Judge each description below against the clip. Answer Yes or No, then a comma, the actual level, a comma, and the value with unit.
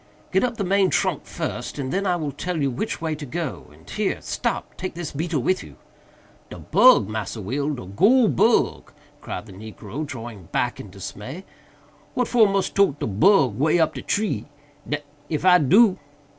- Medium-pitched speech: Yes, medium, 150 Hz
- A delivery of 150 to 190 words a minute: Yes, average, 170 wpm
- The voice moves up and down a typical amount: No, wide, 6.4 semitones